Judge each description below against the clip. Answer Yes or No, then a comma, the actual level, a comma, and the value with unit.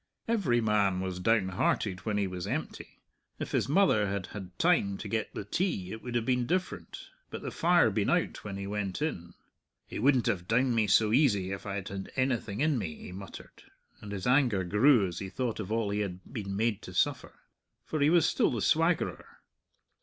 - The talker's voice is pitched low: Yes, low, 105 Hz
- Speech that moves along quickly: Yes, fast, 215 wpm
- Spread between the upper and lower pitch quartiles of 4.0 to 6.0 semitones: Yes, average, 4.9 semitones